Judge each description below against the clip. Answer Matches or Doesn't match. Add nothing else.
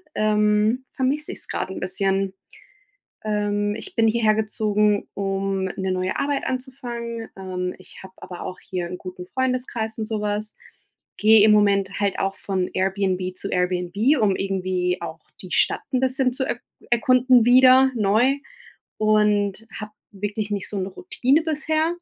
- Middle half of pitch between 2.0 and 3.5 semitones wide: Doesn't match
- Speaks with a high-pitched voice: Matches